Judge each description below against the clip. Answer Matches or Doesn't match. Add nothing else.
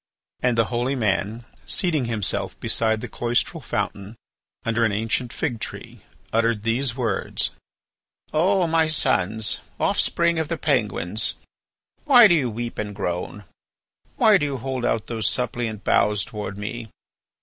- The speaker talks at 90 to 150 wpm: Matches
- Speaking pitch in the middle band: Doesn't match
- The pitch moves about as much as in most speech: Matches